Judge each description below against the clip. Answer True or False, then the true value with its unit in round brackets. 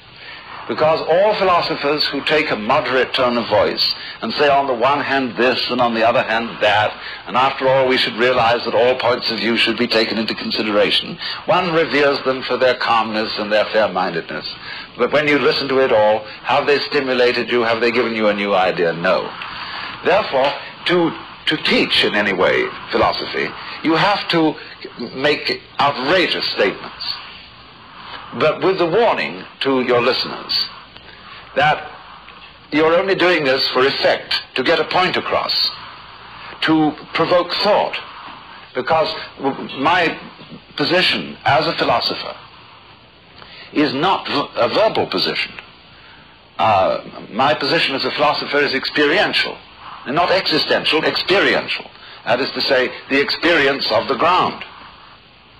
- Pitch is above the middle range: False (135 Hz)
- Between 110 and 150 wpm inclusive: True (145 wpm)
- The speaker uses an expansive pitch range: False (4.1 semitones)